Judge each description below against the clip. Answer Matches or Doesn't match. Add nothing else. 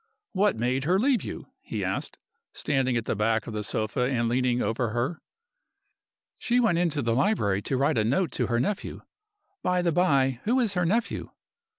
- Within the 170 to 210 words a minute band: Matches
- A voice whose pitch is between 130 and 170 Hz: Matches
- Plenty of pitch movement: Matches